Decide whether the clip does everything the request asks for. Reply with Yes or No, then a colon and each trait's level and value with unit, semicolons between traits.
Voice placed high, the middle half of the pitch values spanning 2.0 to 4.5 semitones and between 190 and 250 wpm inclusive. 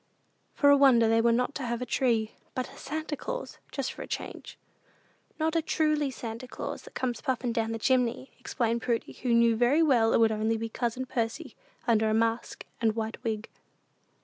Yes: high, 235 Hz; narrow, 2.6 semitones; average, 200 wpm